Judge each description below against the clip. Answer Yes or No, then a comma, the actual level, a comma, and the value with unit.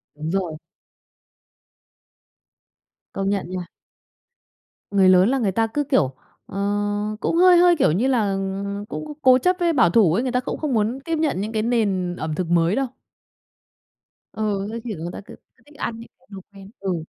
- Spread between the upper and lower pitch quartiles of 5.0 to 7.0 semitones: Yes, wide, 5.5 semitones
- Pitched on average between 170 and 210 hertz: Yes, high, 205 Hz